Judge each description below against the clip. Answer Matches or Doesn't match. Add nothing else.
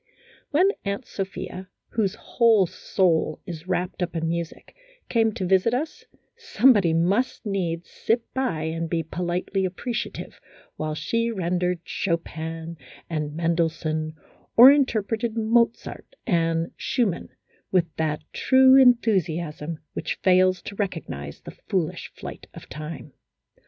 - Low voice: Doesn't match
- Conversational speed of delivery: Doesn't match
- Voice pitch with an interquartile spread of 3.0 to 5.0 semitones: Doesn't match